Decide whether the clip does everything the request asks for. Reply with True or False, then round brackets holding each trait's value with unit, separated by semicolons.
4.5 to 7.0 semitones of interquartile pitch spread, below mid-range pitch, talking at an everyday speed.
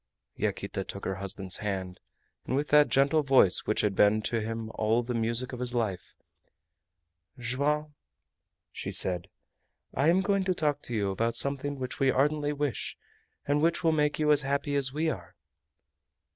True (4.9 semitones; 130 Hz; 170 wpm)